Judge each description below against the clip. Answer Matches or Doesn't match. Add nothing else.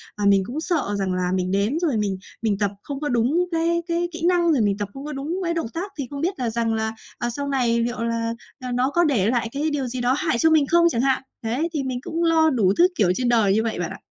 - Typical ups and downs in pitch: Doesn't match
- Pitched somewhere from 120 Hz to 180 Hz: Doesn't match